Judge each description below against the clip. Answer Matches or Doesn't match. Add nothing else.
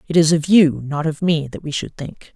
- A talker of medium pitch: Matches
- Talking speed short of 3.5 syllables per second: Doesn't match